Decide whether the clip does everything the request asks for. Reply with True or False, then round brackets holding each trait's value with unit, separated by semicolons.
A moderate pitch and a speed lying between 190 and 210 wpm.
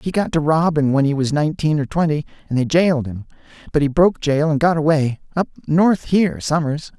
True (150 Hz; 205 wpm)